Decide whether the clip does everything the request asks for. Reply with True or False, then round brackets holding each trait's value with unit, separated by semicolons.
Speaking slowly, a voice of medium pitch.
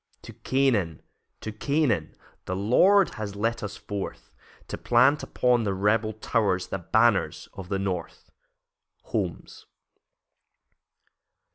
False (115 wpm; 105 Hz)